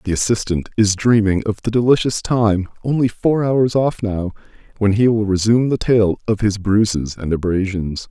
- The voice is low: Yes, low, 105 Hz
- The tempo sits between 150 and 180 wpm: Yes, average, 165 wpm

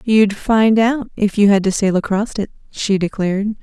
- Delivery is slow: No, average, 200 wpm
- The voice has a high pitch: Yes, high, 205 Hz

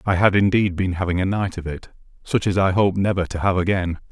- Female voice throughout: No, male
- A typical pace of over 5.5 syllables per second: Yes, 5.9 syllables/s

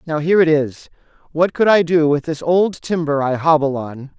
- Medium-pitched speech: Yes, medium, 155 Hz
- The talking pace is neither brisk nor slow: No, fast, 215 wpm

